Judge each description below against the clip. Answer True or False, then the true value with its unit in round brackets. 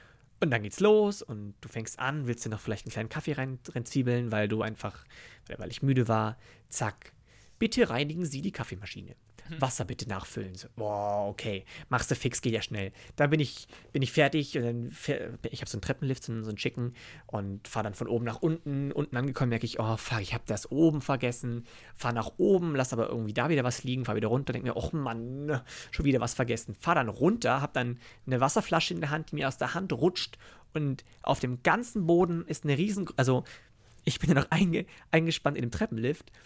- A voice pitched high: False (125 Hz)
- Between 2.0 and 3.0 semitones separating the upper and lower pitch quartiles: False (4.4 semitones)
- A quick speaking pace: True (215 wpm)